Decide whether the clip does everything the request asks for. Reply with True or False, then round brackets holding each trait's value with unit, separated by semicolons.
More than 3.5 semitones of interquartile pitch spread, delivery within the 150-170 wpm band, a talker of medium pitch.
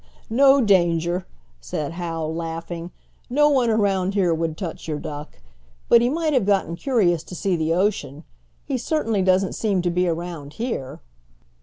True (5.1 semitones; 160 wpm; 180 Hz)